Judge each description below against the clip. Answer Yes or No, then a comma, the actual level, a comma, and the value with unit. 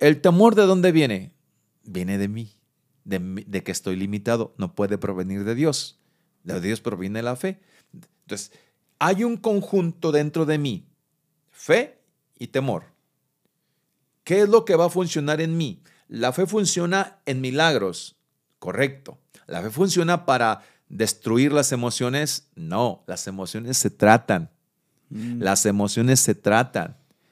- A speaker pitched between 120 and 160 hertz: Yes, medium, 140 Hz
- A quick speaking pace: No, average, 140 wpm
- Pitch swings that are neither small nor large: No, wide, 8.2 semitones